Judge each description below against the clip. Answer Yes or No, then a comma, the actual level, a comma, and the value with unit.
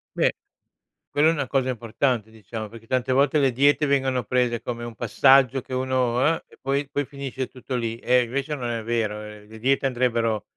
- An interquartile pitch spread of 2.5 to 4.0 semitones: Yes, average, 2.8 semitones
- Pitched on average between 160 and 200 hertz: No, low, 125 Hz